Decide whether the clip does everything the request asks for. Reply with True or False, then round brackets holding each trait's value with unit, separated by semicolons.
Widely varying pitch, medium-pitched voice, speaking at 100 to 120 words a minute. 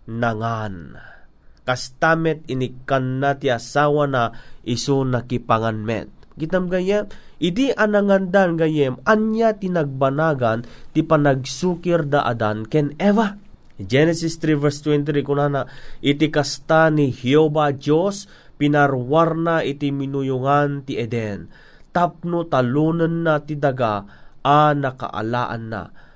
False (4.6 semitones; 145 Hz; 110 wpm)